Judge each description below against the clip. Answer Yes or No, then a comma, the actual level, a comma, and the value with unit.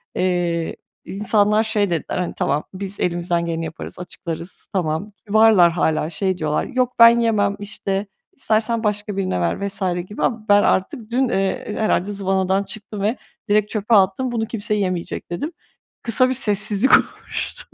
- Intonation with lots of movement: No, average, 3.3 semitones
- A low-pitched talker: No, high, 200 Hz